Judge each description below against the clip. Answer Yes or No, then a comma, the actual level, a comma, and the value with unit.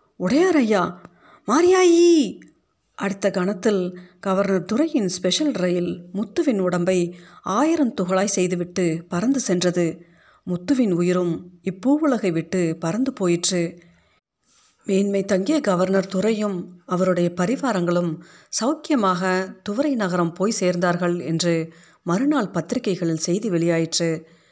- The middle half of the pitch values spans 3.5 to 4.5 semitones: Yes, average, 3.9 semitones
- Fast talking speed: No, average, 95 wpm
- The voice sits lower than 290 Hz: Yes, medium, 185 Hz